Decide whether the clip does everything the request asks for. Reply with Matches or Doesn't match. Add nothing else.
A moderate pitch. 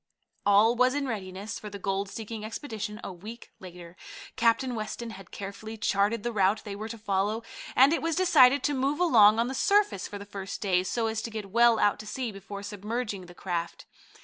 Doesn't match